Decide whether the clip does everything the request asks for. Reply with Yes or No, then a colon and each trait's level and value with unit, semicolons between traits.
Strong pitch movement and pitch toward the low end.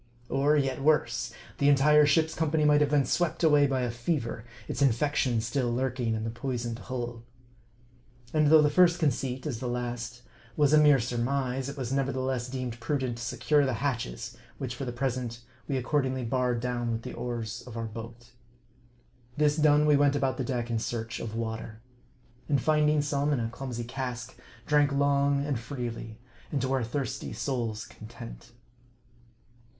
No: average, 3.3 semitones; low, 130 Hz